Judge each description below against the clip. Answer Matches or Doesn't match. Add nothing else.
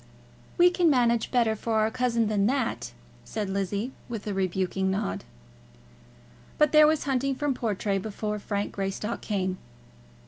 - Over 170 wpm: Doesn't match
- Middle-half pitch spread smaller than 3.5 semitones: Doesn't match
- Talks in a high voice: Matches